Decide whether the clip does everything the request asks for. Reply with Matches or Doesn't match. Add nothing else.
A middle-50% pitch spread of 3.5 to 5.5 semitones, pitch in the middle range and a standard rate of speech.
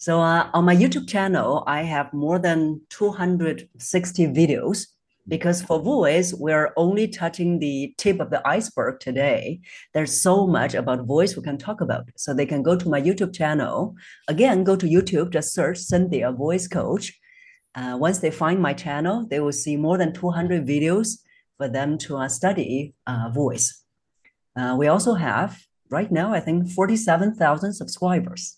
Matches